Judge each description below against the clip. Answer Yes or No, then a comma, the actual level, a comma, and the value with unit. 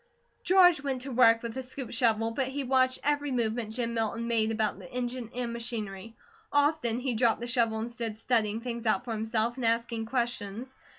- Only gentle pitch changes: Yes, narrow, 2.3 semitones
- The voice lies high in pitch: Yes, high, 235 Hz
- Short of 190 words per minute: No, average, 195 wpm